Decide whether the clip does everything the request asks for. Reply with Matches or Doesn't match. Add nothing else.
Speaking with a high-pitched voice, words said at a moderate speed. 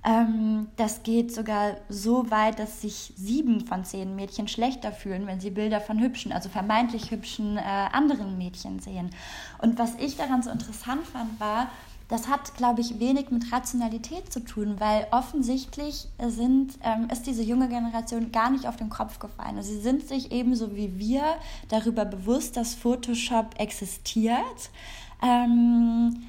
Matches